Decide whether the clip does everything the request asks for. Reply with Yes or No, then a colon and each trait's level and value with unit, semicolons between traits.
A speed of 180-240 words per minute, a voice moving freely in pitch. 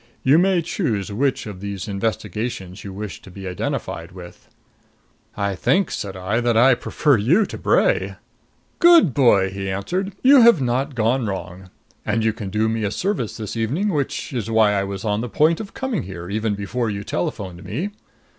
Yes: average, 185 wpm; wide, 6.0 semitones